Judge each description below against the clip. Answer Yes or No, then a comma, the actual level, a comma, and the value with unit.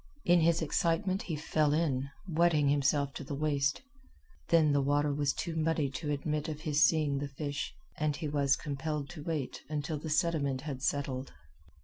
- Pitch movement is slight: Yes, narrow, 2.1 semitones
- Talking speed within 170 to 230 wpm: Yes, average, 175 wpm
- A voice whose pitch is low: No, medium, 150 Hz